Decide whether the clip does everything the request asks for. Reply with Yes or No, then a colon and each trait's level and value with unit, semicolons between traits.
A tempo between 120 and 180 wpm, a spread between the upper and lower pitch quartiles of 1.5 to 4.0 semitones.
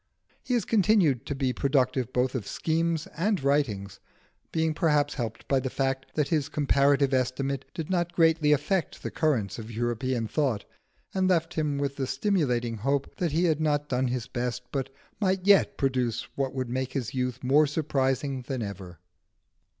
Yes: average, 175 wpm; average, 3.7 semitones